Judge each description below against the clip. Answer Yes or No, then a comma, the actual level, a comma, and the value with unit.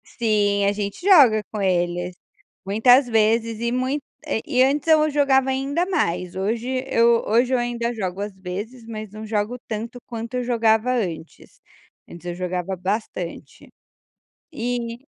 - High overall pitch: Yes, high, 225 Hz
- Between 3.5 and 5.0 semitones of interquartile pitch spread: Yes, average, 3.8 semitones